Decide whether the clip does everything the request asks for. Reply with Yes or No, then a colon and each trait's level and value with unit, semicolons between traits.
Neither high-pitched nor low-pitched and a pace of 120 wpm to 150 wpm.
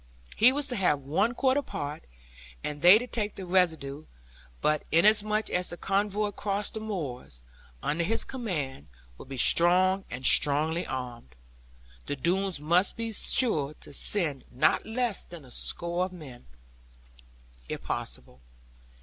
Yes: medium, 175 Hz; average, 145 wpm